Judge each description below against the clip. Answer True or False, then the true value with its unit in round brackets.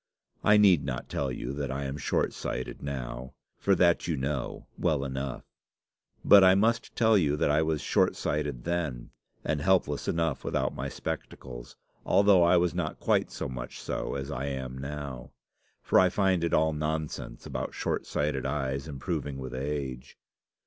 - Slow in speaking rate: False (170 wpm)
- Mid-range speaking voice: False (75 Hz)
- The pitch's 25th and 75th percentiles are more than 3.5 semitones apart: True (4.4 semitones)